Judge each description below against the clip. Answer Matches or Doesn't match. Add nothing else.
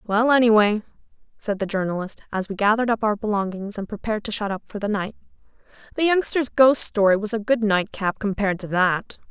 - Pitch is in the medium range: Doesn't match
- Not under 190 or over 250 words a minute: Matches